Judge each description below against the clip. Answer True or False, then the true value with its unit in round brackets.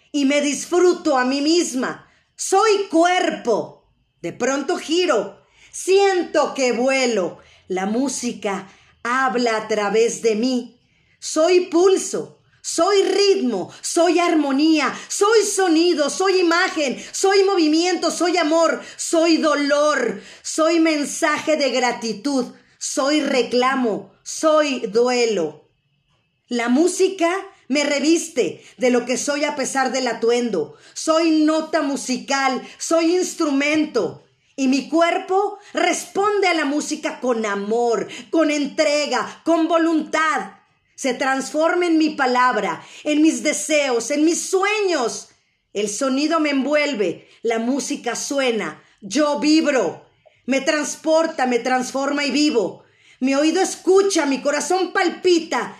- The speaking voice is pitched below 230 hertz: False (295 Hz)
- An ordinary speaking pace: False (115 wpm)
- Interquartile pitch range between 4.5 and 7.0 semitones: True (5.0 semitones)